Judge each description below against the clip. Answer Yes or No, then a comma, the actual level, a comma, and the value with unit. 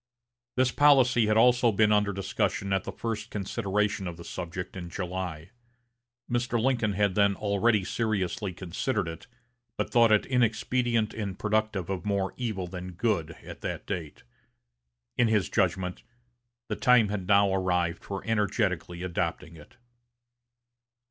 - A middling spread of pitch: Yes, average, 3.4 semitones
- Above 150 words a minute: No, average, 140 wpm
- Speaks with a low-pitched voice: Yes, low, 100 Hz